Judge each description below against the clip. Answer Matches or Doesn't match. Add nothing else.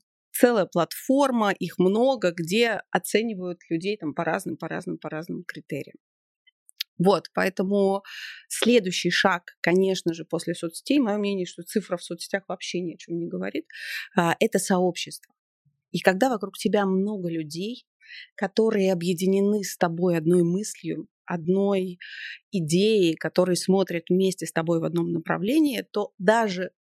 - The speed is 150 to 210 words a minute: Doesn't match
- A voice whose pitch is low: Doesn't match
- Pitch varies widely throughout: Doesn't match